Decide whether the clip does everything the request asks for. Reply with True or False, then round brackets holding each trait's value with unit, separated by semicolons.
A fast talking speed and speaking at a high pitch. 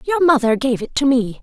True (255 wpm; 260 Hz)